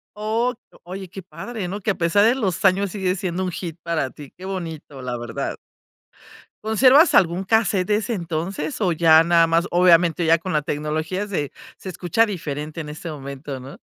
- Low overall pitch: No, medium, 175 Hz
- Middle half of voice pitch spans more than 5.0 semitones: No, average, 3.9 semitones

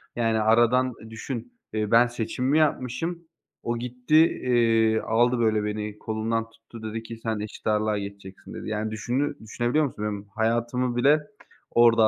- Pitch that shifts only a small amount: Yes, narrow, 2.2 semitones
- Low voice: Yes, low, 115 Hz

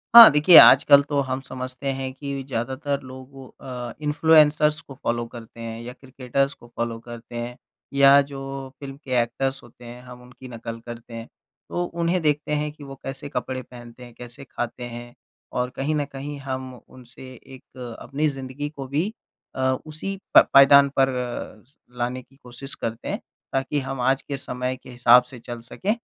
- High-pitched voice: No, low, 130 Hz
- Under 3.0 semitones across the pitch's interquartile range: Yes, narrow, 2.4 semitones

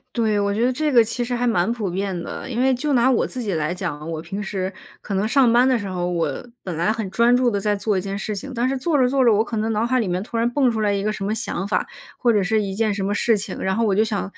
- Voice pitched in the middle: No, high, 215 Hz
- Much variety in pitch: No, average, 3.6 semitones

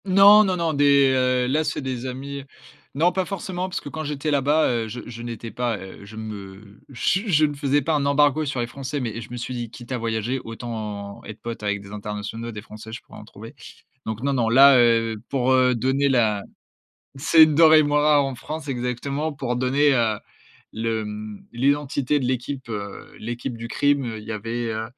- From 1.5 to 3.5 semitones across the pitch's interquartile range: No, average, 4.1 semitones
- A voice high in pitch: No, low, 125 Hz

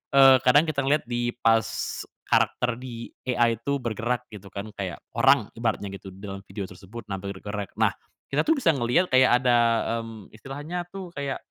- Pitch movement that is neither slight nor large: Yes, average, 4.6 semitones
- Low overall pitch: Yes, low, 120 Hz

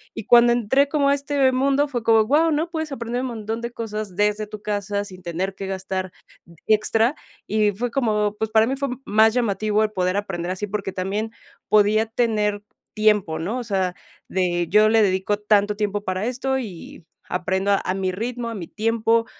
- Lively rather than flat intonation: No, average, 3.3 semitones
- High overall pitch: Yes, high, 215 Hz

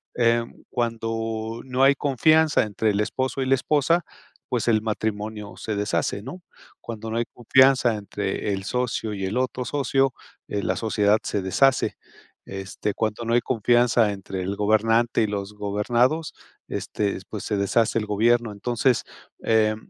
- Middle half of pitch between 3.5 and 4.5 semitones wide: No, average, 3.1 semitones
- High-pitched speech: No, low, 115 Hz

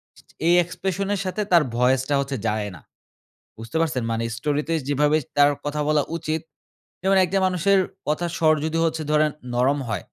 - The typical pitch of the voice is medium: Yes, medium, 150 Hz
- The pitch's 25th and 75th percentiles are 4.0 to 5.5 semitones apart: No, average, 3.6 semitones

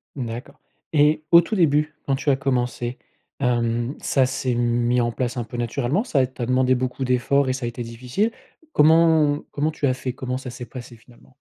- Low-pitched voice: Yes, low, 130 Hz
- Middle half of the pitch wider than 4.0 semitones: No, average, 3.0 semitones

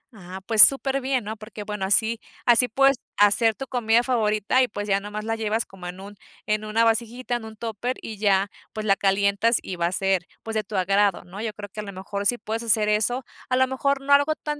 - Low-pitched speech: No, high, 215 Hz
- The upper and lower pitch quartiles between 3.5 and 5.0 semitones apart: No, average, 3.1 semitones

